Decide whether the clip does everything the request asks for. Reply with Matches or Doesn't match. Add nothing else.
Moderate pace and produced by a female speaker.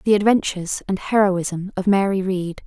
Matches